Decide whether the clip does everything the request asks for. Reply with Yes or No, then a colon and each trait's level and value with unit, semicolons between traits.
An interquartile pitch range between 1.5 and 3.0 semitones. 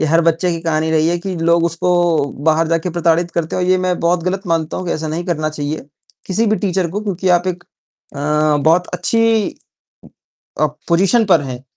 Yes: narrow, 2.5 semitones